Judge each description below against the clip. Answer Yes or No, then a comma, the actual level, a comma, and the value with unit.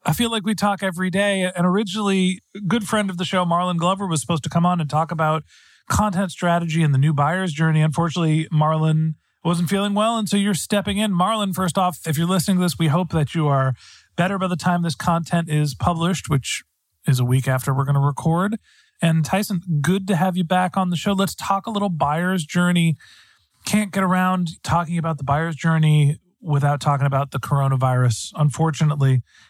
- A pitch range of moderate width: Yes, average, 3.5 semitones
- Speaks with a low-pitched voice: No, medium, 170 Hz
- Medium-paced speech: No, fast, 210 wpm